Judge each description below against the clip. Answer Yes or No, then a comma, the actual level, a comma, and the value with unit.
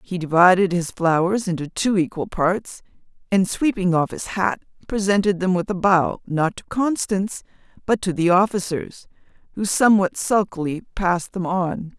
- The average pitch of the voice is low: No, medium, 185 Hz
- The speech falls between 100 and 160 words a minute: Yes, average, 155 wpm